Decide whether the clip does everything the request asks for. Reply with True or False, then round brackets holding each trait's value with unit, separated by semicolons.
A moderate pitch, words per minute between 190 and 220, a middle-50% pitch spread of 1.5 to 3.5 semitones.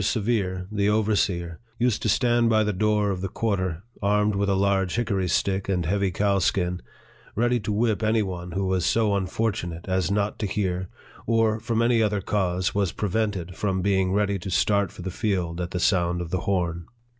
False (100 Hz; 200 wpm; 2.7 semitones)